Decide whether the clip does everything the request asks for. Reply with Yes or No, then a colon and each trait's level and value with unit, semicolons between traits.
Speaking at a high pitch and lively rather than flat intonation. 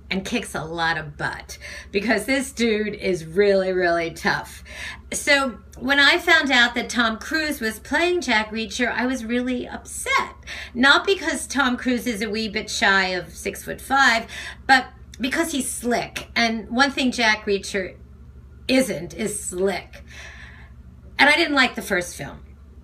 Yes: high, 225 Hz; wide, 6.2 semitones